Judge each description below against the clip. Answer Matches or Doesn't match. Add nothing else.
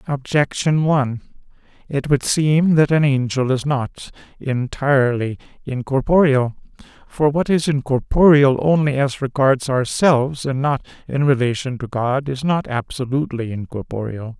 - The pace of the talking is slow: Matches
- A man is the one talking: Matches